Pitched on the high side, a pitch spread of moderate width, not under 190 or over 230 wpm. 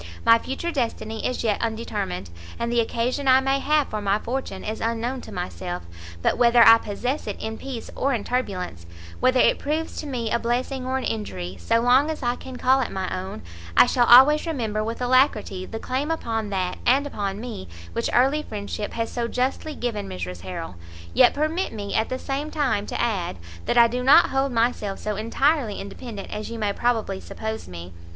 Yes: high, 230 Hz; average, 4.2 semitones; average, 200 wpm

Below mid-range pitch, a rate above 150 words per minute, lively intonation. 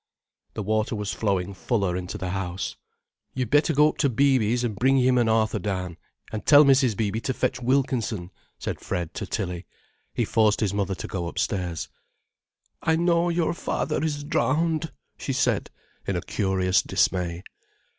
Yes: low, 110 Hz; average, 165 wpm; wide, 6.2 semitones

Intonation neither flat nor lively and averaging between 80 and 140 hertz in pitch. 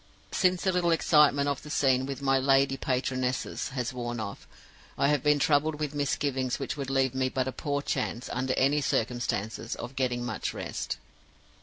No: narrow, 2.2 semitones; low, 135 Hz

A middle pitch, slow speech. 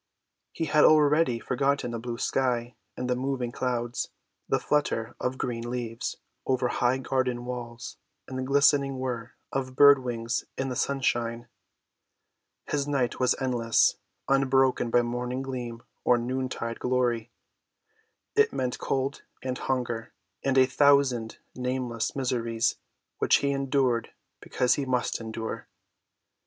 No: low, 125 Hz; slow, 130 wpm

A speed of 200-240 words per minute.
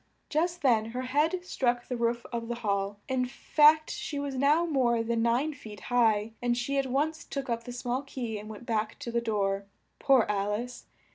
Yes: fast, 205 wpm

